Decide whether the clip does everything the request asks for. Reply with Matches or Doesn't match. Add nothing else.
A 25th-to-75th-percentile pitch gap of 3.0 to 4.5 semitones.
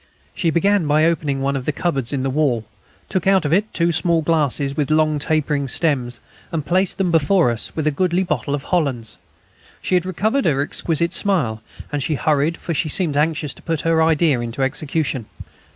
Matches